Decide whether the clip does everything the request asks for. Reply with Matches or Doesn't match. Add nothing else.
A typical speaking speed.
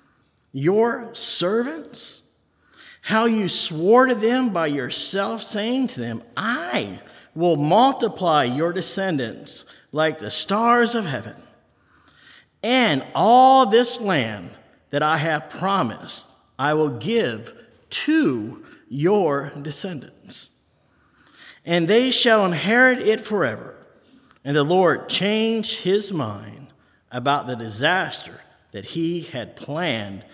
Doesn't match